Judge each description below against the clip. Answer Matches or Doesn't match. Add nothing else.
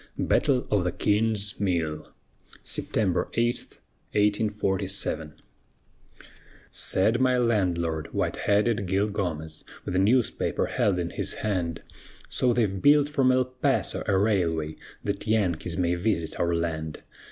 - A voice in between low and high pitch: Doesn't match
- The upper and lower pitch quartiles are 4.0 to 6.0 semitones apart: Matches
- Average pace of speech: Doesn't match